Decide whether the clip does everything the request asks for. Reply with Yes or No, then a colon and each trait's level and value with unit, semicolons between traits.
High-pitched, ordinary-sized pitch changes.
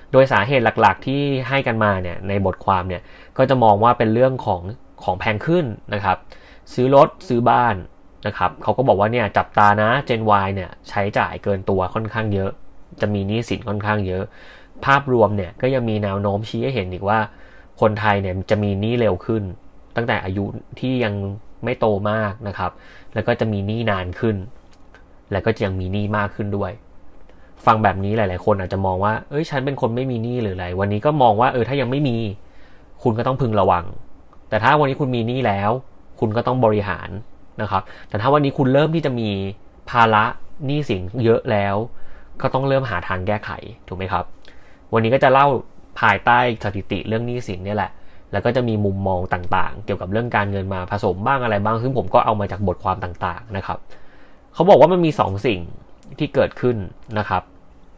No: low, 105 Hz; average, 3.8 semitones